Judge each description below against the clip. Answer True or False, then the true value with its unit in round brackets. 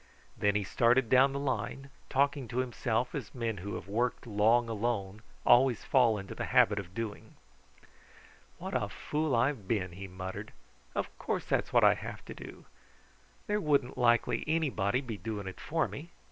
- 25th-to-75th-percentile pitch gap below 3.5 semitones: False (4.4 semitones)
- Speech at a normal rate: True (175 wpm)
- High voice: False (115 Hz)